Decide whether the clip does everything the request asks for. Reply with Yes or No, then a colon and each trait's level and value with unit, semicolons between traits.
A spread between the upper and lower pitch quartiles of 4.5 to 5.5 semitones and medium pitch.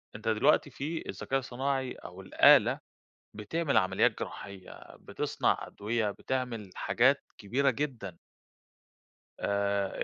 No: average, 5.0 semitones; low, 115 Hz